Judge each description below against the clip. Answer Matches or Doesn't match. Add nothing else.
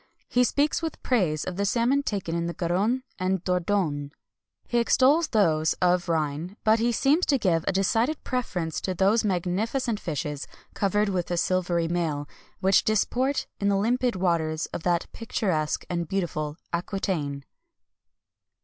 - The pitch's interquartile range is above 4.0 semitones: Matches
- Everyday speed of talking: Matches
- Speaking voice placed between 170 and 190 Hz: Matches